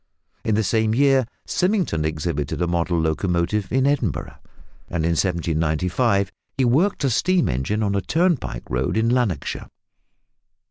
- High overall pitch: No, low, 100 Hz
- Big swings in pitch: Yes, wide, 7.5 semitones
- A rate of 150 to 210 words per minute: No, average, 140 wpm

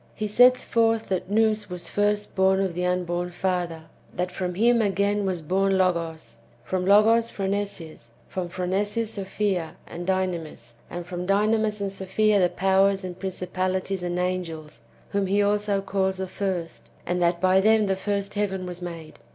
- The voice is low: No, high, 190 Hz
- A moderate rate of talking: Yes, average, 165 wpm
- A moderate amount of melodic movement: No, narrow, 2.3 semitones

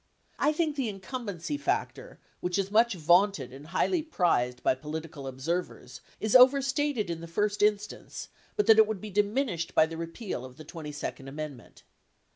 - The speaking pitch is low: No, high, 190 Hz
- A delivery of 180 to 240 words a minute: No, average, 165 wpm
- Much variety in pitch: Yes, wide, 6.6 semitones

